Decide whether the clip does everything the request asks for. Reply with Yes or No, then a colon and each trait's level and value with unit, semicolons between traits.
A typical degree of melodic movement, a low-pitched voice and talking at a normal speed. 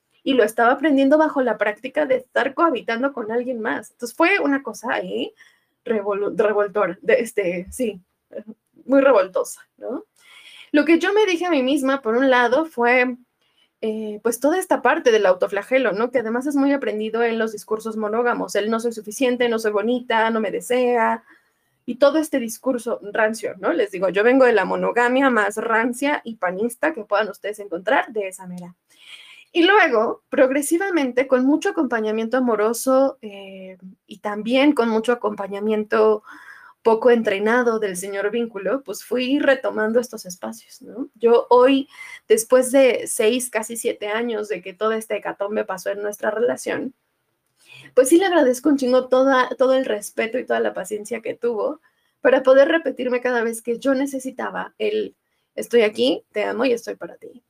No: average, 4.0 semitones; high, 240 Hz; average, 170 wpm